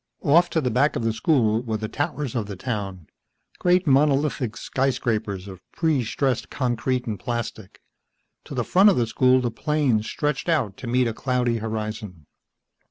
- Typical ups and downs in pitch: Yes, average, 4.6 semitones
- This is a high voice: No, low, 125 Hz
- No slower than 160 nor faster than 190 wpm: Yes, average, 170 wpm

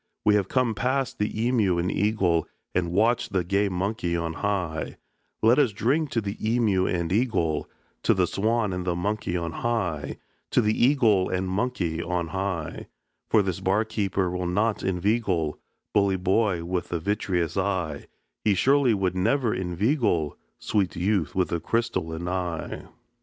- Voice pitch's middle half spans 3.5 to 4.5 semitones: Yes, average, 4.0 semitones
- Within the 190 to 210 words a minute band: No, average, 160 wpm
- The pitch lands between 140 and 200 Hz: No, very low, 95 Hz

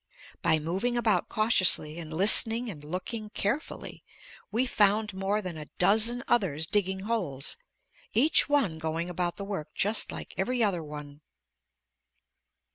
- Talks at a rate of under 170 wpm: Yes, slow, 135 wpm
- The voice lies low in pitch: No, high, 195 Hz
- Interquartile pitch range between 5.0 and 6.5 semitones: Yes, wide, 5.4 semitones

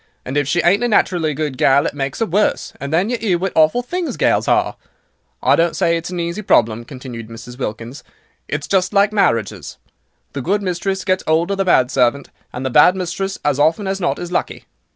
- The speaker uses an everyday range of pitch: No, wide, 5.9 semitones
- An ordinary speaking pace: No, fast, 215 wpm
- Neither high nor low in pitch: Yes, medium, 170 Hz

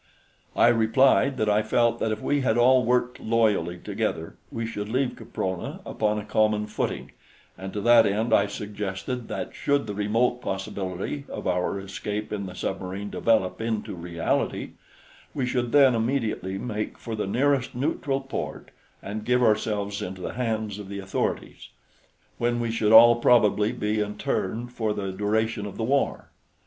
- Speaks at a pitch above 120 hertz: No, low, 110 Hz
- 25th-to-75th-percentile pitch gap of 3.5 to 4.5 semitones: No, average, 2.9 semitones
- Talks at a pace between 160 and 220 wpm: Yes, average, 165 wpm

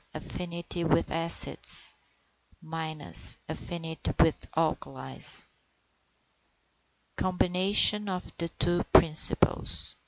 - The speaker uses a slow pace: Yes, slow, 65 wpm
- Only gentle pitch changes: Yes, narrow, 1.8 semitones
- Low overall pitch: No, medium, 170 Hz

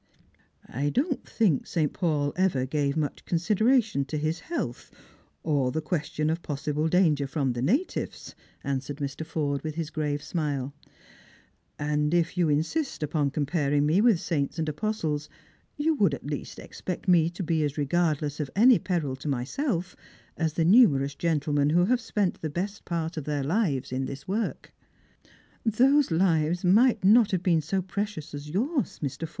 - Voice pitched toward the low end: No, medium, 160 Hz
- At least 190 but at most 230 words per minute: No, average, 170 wpm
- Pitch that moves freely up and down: No, average, 4.5 semitones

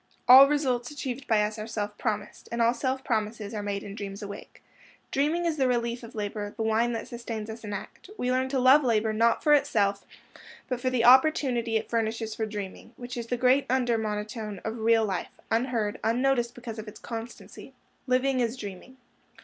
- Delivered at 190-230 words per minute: Yes, average, 200 wpm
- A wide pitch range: No, average, 3.0 semitones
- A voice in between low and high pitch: No, high, 230 Hz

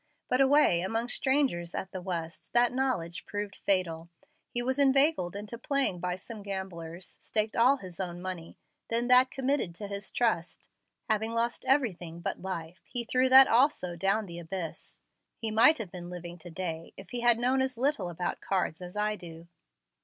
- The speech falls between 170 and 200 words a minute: Yes, average, 180 wpm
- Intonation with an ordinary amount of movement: No, wide, 5.8 semitones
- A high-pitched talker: Yes, high, 200 Hz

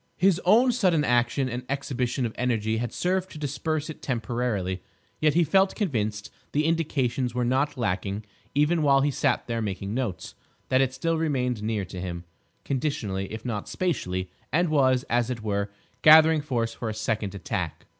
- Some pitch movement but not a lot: No, wide, 5.7 semitones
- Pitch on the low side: Yes, low, 125 Hz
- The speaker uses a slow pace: No, average, 165 wpm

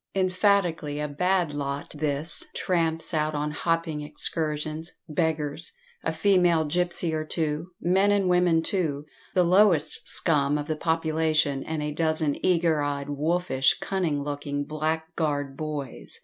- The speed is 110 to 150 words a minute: Yes, slow, 135 wpm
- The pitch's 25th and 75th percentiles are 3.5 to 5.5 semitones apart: No, average, 2.7 semitones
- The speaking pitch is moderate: Yes, medium, 155 Hz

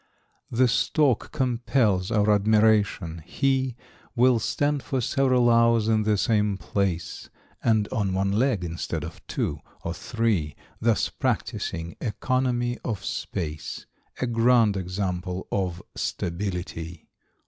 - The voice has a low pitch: Yes, low, 105 Hz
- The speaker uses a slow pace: Yes, slow, 120 wpm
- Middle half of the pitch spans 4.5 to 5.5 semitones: Yes, average, 4.9 semitones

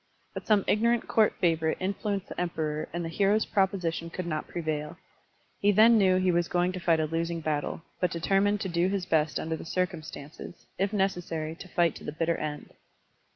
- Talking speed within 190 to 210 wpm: Yes, average, 200 wpm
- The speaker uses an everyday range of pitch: Yes, average, 3.2 semitones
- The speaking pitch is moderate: Yes, medium, 175 Hz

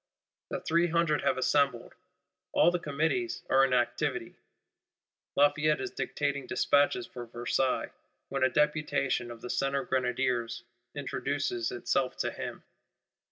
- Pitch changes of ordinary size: Yes, average, 3.0 semitones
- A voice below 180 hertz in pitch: Yes, low, 135 Hz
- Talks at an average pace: No, slow, 125 wpm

